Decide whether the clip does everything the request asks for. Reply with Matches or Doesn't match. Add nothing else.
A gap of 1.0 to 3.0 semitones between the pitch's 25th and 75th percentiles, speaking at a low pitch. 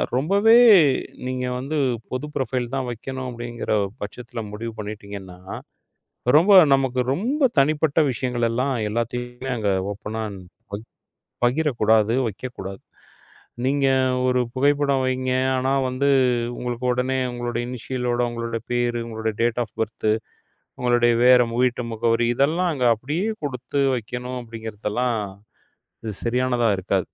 Matches